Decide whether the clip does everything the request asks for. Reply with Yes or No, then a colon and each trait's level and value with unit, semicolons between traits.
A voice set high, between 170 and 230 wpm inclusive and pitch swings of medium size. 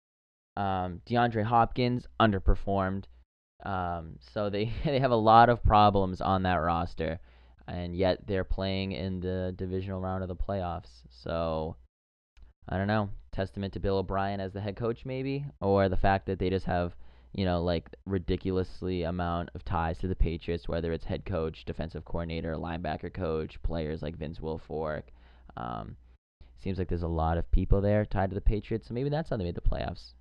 No: very low, 90 Hz; average, 180 wpm; average, 3.2 semitones